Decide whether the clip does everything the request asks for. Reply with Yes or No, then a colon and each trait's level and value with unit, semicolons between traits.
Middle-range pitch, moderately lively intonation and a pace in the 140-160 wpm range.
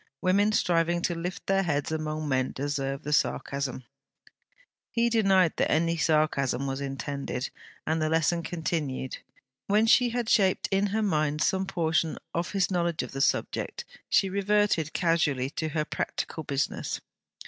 Yes: medium, 165 Hz; average, 4.8 semitones; average, 150 wpm